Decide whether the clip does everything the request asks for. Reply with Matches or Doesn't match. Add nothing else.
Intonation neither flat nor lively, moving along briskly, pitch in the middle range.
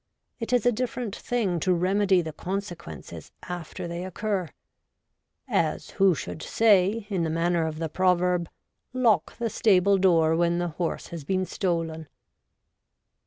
Doesn't match